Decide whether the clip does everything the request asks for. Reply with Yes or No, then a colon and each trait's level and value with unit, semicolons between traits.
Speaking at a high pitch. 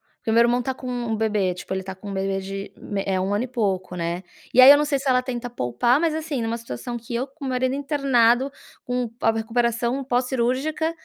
Yes: high, 240 Hz